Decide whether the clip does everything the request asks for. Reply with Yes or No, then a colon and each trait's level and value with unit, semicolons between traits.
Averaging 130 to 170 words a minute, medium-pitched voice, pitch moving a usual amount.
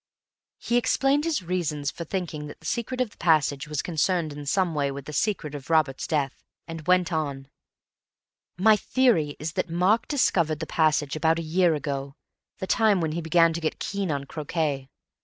No: average, 185 wpm; medium, 160 Hz; average, 3.8 semitones